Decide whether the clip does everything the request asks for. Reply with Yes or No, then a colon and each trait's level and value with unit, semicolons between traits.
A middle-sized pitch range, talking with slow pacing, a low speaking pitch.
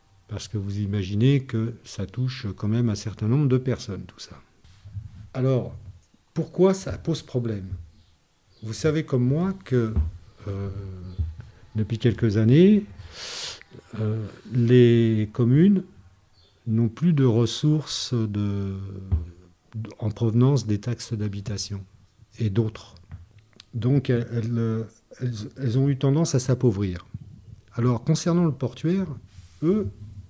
Yes: average, 3.9 semitones; slow, 120 wpm; low, 110 Hz